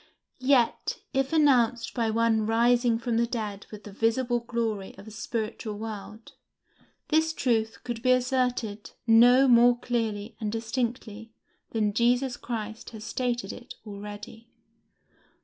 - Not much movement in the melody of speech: Yes, narrow, 2.0 semitones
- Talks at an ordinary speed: No, slow, 130 wpm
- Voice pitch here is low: No, high, 230 Hz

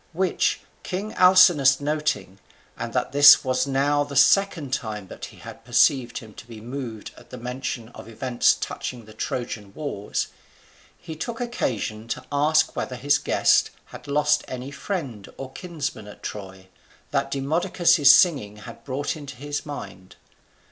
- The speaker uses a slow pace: No, average, 155 wpm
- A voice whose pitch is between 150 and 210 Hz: No, low, 135 Hz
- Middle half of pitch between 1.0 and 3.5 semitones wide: No, average, 4.7 semitones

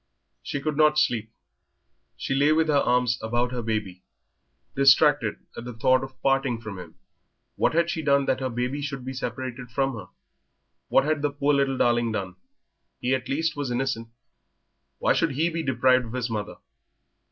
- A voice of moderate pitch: No, low, 130 Hz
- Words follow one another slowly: No, average, 180 wpm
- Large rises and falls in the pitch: No, average, 3.0 semitones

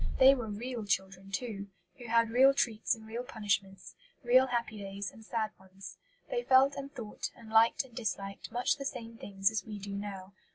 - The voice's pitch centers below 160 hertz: No, high, 220 Hz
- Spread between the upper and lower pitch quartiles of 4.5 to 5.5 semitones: No, average, 3.7 semitones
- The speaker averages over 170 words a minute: Yes, average, 195 wpm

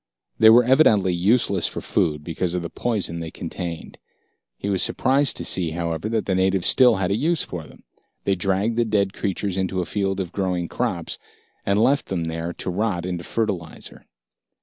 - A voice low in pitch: Yes, very low, 95 Hz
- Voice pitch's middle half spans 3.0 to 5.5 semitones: Yes, average, 3.8 semitones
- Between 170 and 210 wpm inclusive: Yes, average, 190 wpm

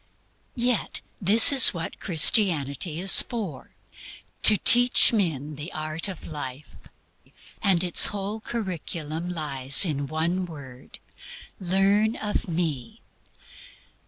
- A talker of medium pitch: Yes, medium, 175 Hz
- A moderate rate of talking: No, slow, 105 wpm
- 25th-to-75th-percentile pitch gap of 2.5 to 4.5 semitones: No, average, 5.1 semitones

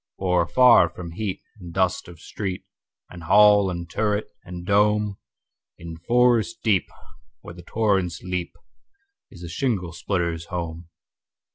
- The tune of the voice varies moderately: Yes, average, 3.4 semitones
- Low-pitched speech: Yes, very low, 90 Hz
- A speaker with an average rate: No, slow, 120 wpm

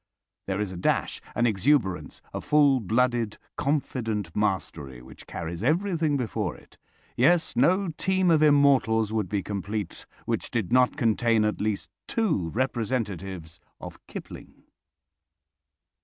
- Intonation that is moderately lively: No, wide, 6.5 semitones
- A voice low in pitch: Yes, low, 115 Hz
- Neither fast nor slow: No, slow, 125 wpm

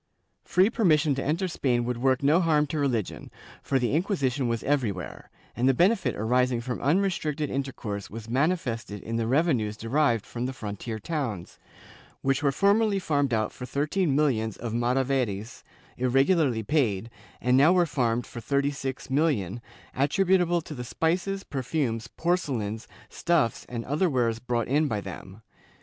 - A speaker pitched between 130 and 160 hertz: Yes, low, 135 Hz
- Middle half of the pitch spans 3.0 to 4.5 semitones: No, average, 4.9 semitones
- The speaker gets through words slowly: No, average, 160 wpm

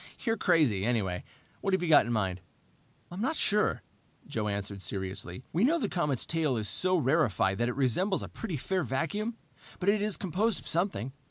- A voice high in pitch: No, medium, 155 Hz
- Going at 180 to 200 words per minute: Yes, average, 190 wpm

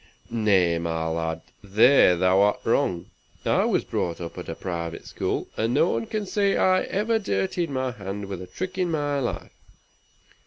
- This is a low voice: Yes, low, 105 Hz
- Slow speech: No, average, 170 wpm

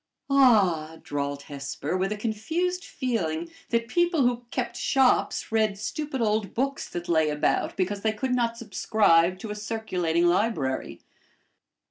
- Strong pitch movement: Yes, wide, 6.0 semitones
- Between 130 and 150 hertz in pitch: No, high, 210 Hz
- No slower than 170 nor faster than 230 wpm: No, average, 140 wpm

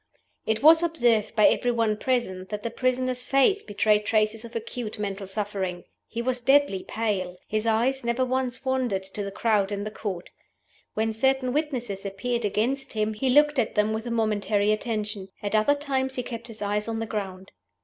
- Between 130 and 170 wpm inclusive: No, average, 190 wpm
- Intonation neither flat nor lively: Yes, average, 3.5 semitones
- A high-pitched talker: Yes, high, 225 Hz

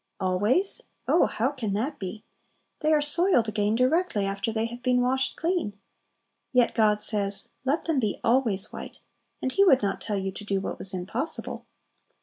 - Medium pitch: No, high, 230 Hz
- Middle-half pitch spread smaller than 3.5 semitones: No, average, 4.9 semitones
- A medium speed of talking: Yes, average, 175 wpm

